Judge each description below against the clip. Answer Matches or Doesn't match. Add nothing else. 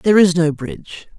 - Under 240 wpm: Matches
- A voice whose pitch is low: Doesn't match